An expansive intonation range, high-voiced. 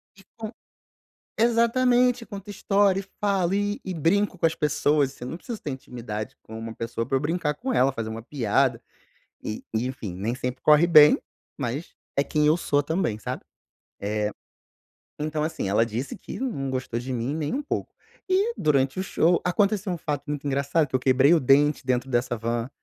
No: wide, 7.0 semitones; medium, 145 Hz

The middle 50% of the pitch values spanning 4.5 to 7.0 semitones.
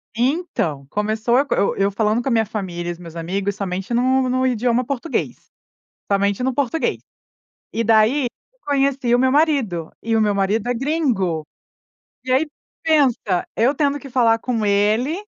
Yes: average, 4.8 semitones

